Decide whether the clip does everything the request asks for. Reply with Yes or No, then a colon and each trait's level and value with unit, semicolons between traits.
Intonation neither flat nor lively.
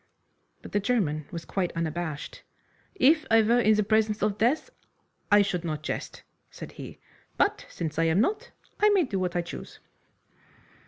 No: wide, 5.9 semitones